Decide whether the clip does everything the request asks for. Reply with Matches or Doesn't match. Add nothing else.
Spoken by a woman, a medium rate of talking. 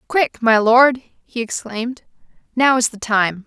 Matches